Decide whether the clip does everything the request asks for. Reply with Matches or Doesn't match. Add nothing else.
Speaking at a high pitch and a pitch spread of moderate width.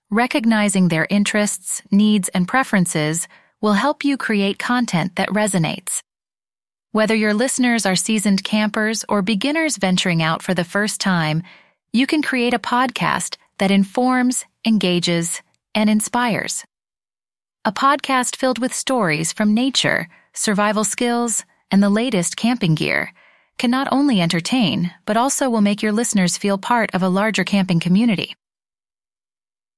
Matches